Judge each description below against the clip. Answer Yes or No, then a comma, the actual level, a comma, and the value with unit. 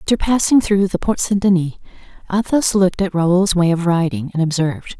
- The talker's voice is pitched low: No, medium, 185 Hz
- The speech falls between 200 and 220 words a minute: No, average, 190 wpm